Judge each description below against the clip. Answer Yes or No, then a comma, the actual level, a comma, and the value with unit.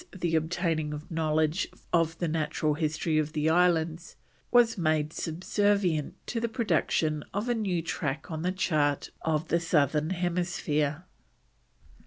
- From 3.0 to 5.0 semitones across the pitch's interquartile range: No, narrow, 2.6 semitones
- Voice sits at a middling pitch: Yes, medium, 160 Hz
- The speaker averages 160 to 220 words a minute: No, average, 140 wpm